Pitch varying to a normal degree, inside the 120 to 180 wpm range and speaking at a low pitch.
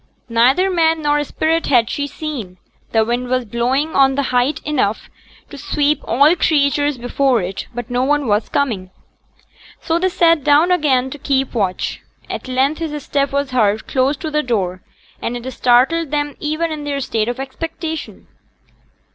No: average, 3.7 semitones; average, 170 wpm; very high, 275 Hz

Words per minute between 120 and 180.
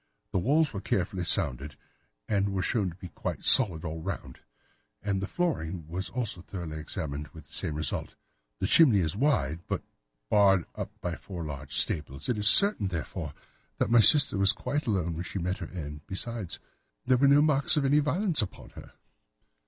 No: average, 190 wpm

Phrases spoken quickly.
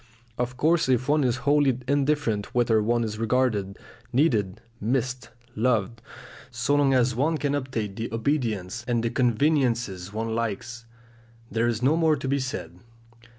No: average, 150 wpm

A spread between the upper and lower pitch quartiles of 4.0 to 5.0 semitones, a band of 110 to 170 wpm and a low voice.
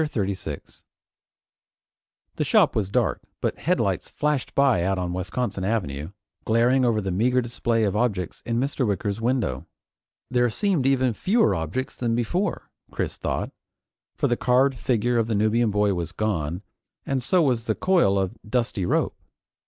Yes: average, 4.5 semitones; average, 160 wpm; low, 115 Hz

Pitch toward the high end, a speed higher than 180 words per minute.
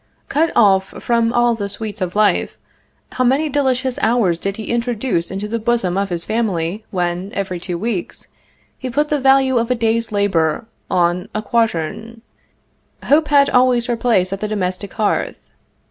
No: high, 220 Hz; average, 170 wpm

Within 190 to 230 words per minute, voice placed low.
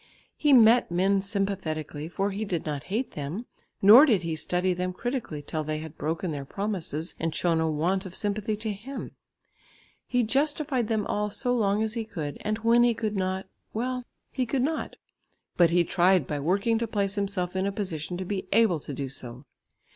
No: average, 195 wpm; high, 195 Hz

